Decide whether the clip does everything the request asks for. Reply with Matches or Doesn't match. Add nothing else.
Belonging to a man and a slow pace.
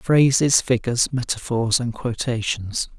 Matches